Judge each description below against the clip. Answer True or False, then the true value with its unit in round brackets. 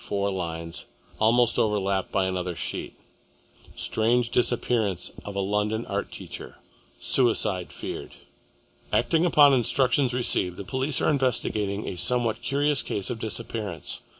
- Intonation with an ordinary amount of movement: True (4.0 semitones)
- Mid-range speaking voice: False (110 Hz)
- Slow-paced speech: True (125 wpm)